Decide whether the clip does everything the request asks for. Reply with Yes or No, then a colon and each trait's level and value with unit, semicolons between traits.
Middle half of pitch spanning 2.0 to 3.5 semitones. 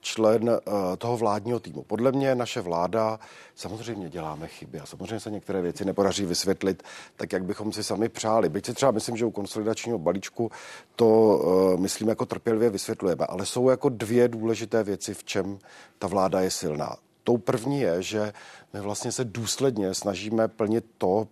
Yes: average, 2.8 semitones